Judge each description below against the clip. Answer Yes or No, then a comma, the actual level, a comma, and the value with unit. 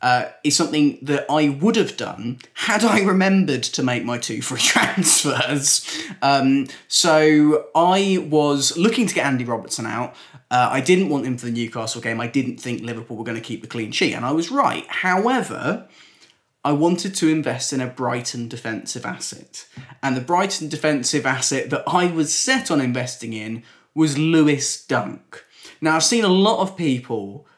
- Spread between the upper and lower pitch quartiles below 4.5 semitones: No, wide, 5.5 semitones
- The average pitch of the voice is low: No, medium, 145 Hz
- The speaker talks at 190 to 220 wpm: No, average, 180 wpm